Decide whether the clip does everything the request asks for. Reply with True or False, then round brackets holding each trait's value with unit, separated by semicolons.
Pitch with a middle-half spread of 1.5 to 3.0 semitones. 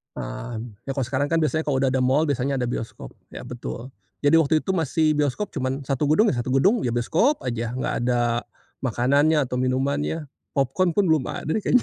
False (3.9 semitones)